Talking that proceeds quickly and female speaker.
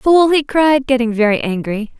No: average, 180 wpm; female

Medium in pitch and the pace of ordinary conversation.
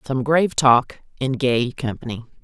No: low, 130 Hz; average, 150 wpm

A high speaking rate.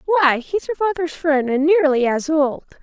No: average, 190 wpm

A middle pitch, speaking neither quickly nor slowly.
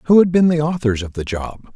No: medium, 145 Hz; fast, 275 wpm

